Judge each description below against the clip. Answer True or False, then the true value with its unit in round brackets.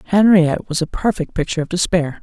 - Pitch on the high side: False (170 Hz)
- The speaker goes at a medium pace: True (190 wpm)